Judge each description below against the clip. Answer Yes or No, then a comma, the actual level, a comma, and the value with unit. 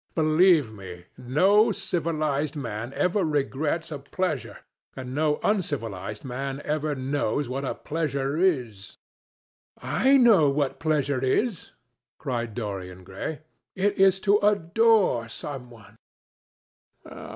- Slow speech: Yes, slow, 115 wpm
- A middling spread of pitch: No, wide, 6.0 semitones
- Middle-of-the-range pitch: Yes, medium, 145 Hz